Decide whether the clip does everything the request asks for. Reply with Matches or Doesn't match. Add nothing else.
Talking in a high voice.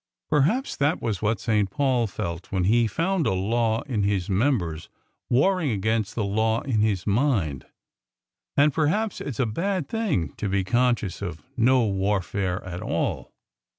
Doesn't match